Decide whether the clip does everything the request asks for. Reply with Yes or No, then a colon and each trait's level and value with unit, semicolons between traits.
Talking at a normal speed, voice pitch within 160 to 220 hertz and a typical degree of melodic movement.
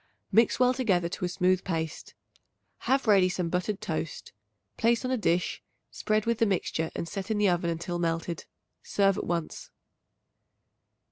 Yes: average, 160 wpm; medium, 185 Hz; average, 4.0 semitones